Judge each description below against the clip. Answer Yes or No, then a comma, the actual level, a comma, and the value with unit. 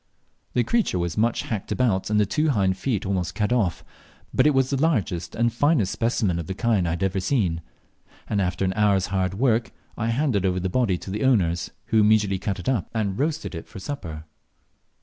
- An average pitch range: Yes, average, 4.2 semitones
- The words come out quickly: Yes, fast, 210 wpm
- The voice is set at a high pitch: No, low, 105 Hz